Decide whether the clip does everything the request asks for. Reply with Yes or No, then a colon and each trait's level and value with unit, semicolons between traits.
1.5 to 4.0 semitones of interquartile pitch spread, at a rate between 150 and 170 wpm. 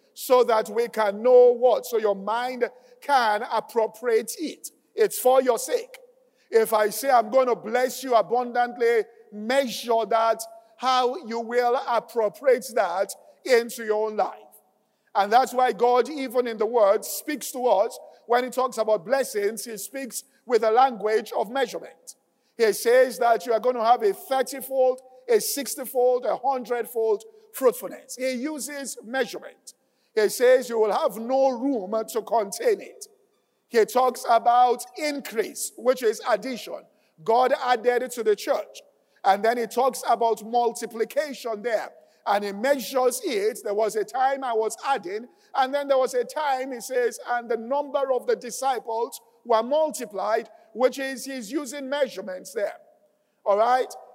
Yes: average, 3.5 semitones; average, 160 wpm